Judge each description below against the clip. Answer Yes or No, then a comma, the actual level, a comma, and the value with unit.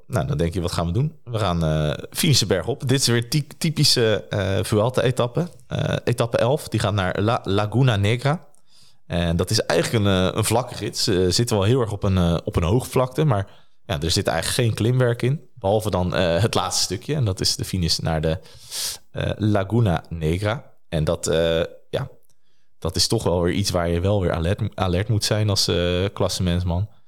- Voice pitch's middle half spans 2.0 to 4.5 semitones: No, average, 5.1 semitones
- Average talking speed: No, fast, 205 wpm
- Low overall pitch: Yes, low, 105 Hz